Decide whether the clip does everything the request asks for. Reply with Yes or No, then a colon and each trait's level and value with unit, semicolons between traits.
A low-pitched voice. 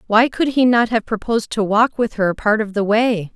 No: high, 220 Hz